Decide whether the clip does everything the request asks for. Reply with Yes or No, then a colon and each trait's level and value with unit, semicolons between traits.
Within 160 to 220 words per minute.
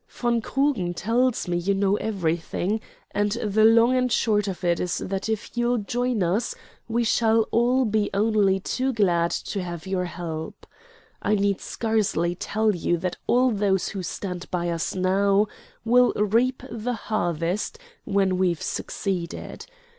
No: average, 150 wpm